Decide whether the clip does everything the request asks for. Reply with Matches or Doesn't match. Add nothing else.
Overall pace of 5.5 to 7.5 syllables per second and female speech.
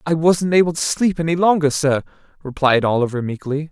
Doesn't match